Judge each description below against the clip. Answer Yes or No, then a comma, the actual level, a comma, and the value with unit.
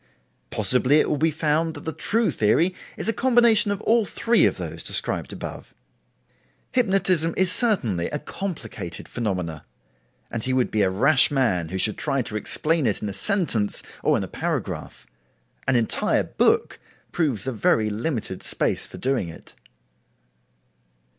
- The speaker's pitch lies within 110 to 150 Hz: Yes, low, 135 Hz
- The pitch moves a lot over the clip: Yes, wide, 9.0 semitones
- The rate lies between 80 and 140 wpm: No, average, 160 wpm